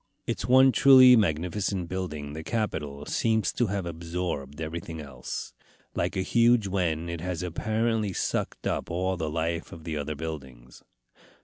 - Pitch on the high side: No, very low, 85 Hz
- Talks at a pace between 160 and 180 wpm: No, average, 150 wpm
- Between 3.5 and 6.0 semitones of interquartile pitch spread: Yes, average, 4.8 semitones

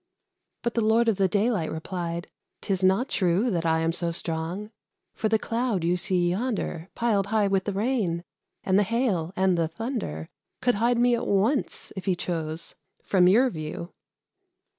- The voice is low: No, high, 190 Hz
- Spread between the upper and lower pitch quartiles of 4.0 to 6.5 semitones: Yes, average, 4.8 semitones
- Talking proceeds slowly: No, average, 175 wpm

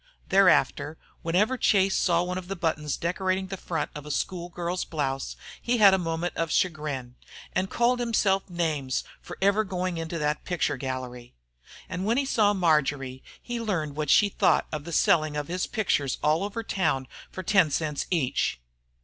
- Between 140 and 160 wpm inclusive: No, average, 175 wpm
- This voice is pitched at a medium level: Yes, medium, 170 Hz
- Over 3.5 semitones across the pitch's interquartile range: Yes, average, 4.4 semitones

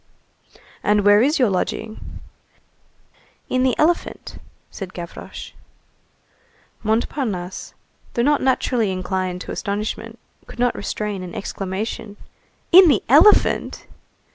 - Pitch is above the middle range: Yes, high, 215 Hz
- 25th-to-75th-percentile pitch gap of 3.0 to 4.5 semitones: No, average, 5.2 semitones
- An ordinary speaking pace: No, slow, 105 wpm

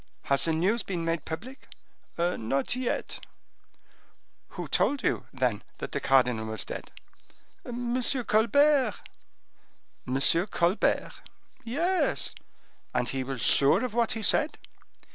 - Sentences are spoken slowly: Yes, slow, 120 wpm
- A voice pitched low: No, high, 190 Hz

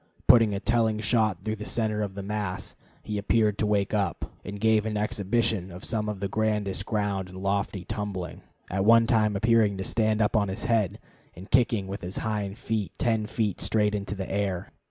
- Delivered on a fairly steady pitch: Yes, narrow, 1.9 semitones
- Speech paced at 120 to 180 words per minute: No, average, 200 wpm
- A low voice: Yes, low, 105 Hz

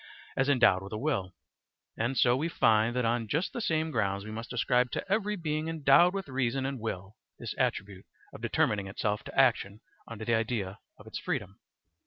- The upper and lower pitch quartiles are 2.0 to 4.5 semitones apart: No, average, 5.2 semitones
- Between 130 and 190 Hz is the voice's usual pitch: No, low, 120 Hz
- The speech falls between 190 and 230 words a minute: Yes, average, 195 wpm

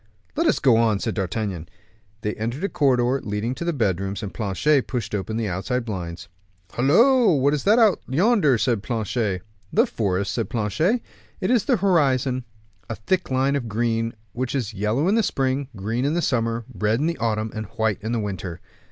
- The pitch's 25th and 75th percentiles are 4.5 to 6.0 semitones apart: Yes, average, 5.0 semitones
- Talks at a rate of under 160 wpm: No, average, 195 wpm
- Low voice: Yes, low, 120 Hz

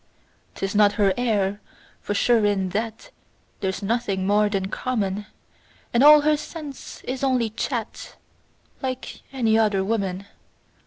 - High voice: Yes, high, 215 Hz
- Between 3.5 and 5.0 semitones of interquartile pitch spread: Yes, average, 3.8 semitones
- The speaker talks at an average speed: No, slow, 130 wpm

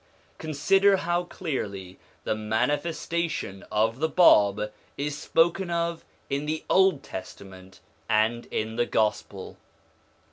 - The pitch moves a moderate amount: No, wide, 7.9 semitones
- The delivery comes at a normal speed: No, slow, 110 wpm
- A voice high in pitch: No, medium, 140 Hz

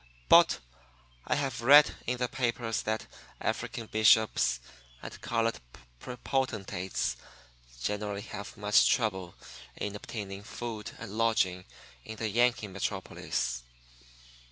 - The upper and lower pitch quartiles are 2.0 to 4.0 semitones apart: Yes, average, 2.8 semitones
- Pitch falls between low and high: No, low, 110 Hz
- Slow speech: Yes, slow, 105 wpm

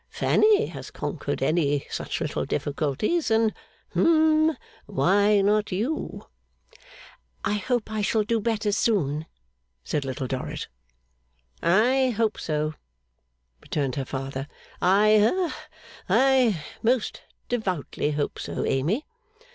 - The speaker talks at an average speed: No, slow, 110 wpm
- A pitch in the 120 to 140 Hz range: No, high, 210 Hz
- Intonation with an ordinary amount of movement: No, wide, 8.1 semitones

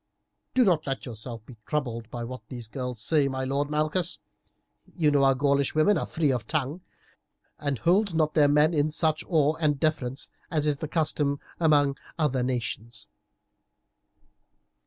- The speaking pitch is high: No, medium, 145 Hz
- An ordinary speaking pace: Yes, average, 165 wpm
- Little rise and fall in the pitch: No, average, 3.3 semitones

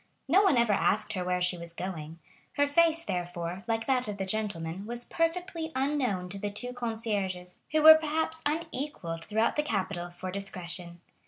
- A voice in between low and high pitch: No, high, 210 Hz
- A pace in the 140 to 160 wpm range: No, average, 175 wpm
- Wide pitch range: Yes, wide, 8.2 semitones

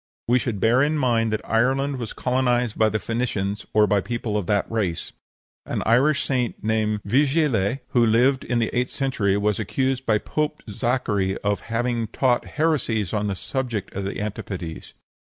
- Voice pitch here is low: Yes, low, 115 Hz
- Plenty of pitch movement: No, average, 3.6 semitones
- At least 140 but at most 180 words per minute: Yes, average, 175 wpm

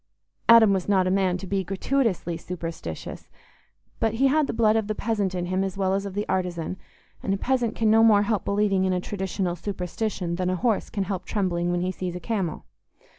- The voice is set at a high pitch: Yes, high, 195 Hz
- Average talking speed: No, fast, 220 wpm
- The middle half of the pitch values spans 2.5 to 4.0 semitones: Yes, average, 2.9 semitones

